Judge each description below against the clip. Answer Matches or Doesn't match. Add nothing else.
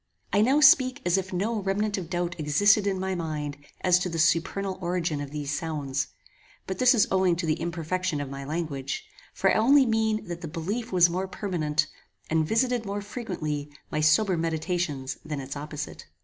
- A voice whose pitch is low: Doesn't match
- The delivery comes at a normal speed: Matches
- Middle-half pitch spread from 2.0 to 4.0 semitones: Doesn't match